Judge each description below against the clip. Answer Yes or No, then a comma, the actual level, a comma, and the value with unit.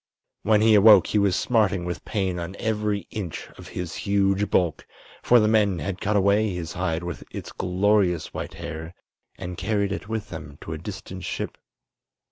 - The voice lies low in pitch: Yes, very low, 95 Hz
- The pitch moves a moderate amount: Yes, average, 3.0 semitones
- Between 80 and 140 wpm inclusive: No, average, 180 wpm